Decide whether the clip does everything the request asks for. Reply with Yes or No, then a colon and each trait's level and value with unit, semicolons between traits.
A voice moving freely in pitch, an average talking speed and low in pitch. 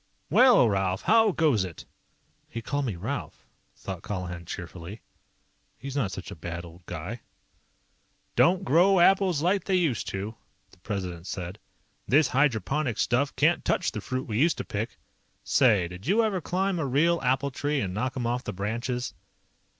Yes: wide, 8.5 semitones; average, 165 wpm; low, 125 Hz